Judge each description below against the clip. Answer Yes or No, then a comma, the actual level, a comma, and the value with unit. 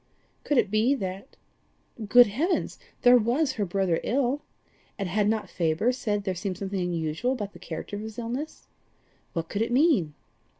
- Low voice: No, high, 210 Hz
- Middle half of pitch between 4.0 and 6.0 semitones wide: Yes, average, 4.7 semitones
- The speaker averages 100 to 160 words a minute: No, average, 170 wpm